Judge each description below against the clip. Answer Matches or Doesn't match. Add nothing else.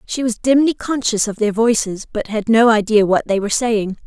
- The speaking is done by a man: Doesn't match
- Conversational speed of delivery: Doesn't match